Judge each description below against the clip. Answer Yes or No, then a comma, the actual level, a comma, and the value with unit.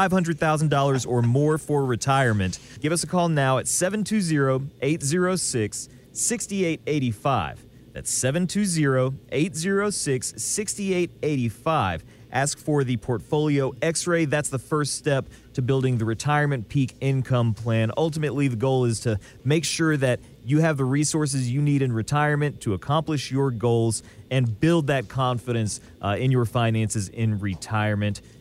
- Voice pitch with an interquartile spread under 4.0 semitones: No, average, 4.3 semitones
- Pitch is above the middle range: No, low, 135 Hz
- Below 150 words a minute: Yes, slow, 135 wpm